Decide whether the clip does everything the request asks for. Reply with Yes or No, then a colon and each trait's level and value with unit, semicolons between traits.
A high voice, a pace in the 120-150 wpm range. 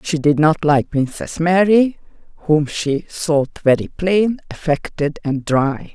No: medium, 160 Hz; average, 140 wpm